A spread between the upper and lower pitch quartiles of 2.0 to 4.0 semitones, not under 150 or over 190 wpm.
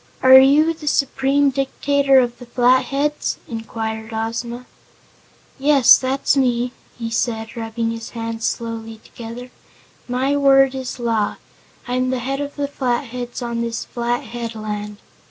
No: average, 2.9 semitones; slow, 135 wpm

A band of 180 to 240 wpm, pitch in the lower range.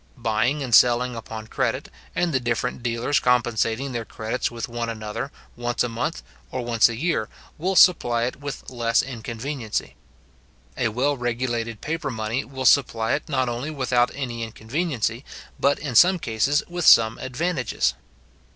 No: average, 155 wpm; low, 120 Hz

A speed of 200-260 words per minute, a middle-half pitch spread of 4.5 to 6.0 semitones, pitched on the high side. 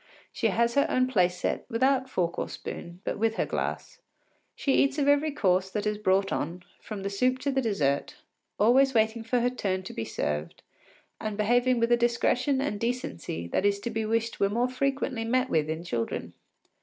Yes: fast, 205 wpm; average, 5.1 semitones; high, 225 Hz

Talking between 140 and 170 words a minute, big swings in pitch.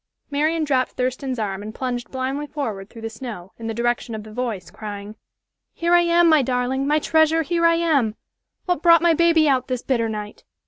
No: average, 200 wpm; wide, 6.0 semitones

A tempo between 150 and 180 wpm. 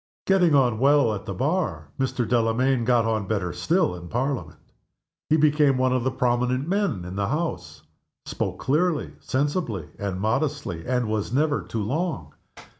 Yes: average, 160 wpm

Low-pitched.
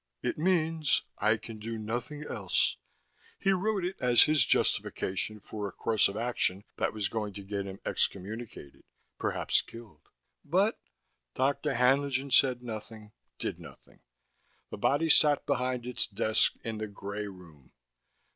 Yes: low, 115 Hz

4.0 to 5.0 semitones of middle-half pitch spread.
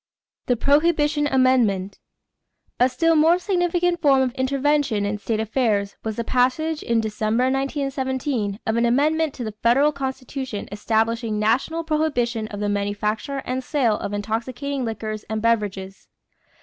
Yes: average, 4.7 semitones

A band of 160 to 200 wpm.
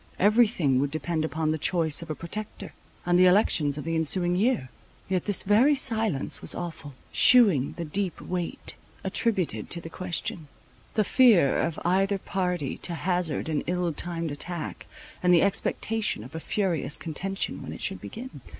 Yes: average, 170 wpm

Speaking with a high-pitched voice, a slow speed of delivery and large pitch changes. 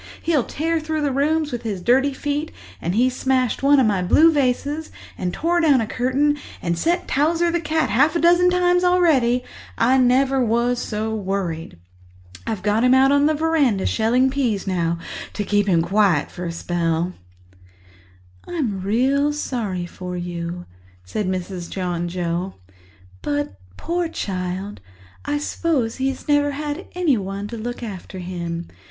No: high, 245 Hz; average, 160 wpm; wide, 7.8 semitones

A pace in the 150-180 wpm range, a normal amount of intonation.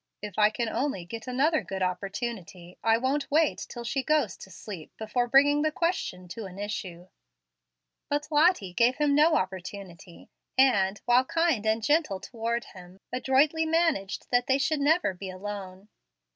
No: average, 160 wpm; wide, 7.0 semitones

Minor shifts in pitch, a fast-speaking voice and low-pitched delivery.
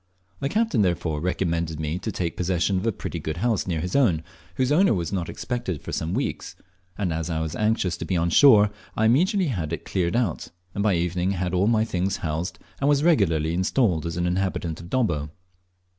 No: average, 5.0 semitones; fast, 210 wpm; very low, 90 Hz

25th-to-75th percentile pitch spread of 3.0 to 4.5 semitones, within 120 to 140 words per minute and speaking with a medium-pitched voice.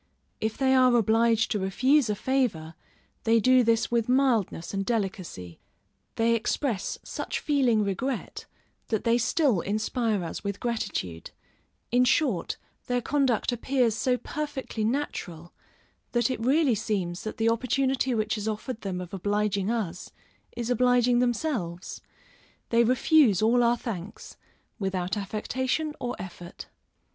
No: average, 4.0 semitones; slow, 135 wpm; high, 230 Hz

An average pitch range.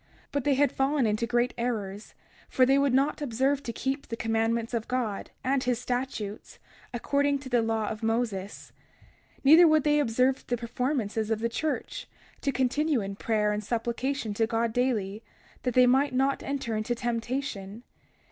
Yes: average, 3.3 semitones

